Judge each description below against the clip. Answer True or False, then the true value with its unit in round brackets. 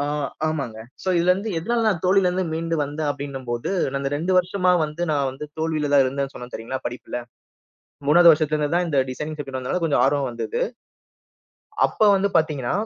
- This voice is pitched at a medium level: True (150 Hz)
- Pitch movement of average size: True (4.0 semitones)